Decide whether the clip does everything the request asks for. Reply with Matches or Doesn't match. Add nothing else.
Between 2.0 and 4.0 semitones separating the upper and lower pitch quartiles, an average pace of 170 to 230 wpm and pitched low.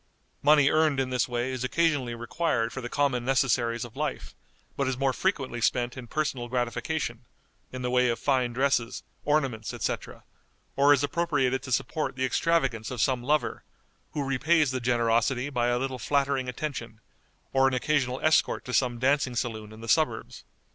Matches